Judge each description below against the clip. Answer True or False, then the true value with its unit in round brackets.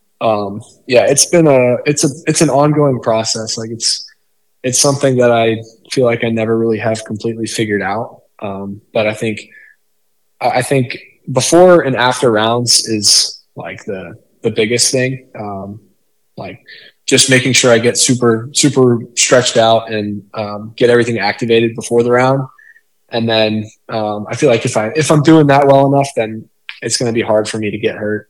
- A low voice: True (115 Hz)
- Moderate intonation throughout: True (3.0 semitones)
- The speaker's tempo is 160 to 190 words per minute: True (180 wpm)